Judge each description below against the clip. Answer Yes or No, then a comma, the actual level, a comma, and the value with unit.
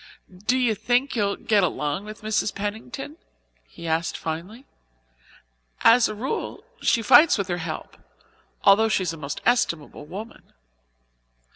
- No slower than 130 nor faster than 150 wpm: Yes, average, 140 wpm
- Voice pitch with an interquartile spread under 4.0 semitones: No, average, 5.3 semitones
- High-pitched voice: Yes, high, 205 Hz